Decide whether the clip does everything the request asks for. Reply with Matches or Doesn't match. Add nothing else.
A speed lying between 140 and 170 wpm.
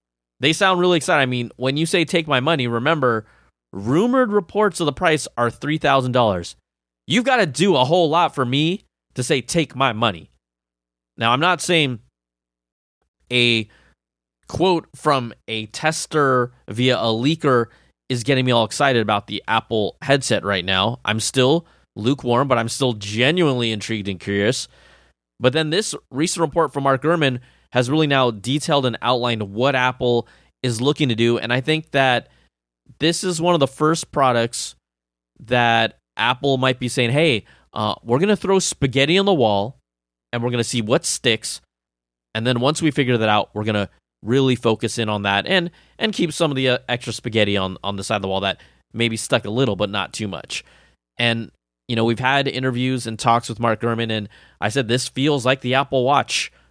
Doesn't match